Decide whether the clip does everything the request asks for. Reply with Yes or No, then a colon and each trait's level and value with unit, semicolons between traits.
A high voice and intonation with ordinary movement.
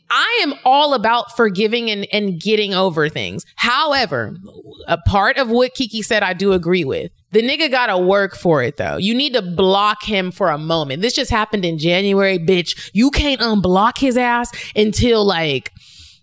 Yes: high, 210 Hz; average, 4.5 semitones